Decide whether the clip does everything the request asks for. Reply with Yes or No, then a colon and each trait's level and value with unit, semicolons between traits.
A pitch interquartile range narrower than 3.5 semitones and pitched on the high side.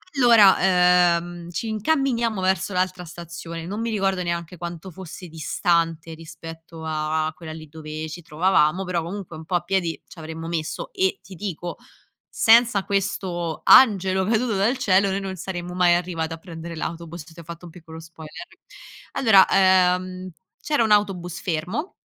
No: average, 2.8 semitones; medium, 175 Hz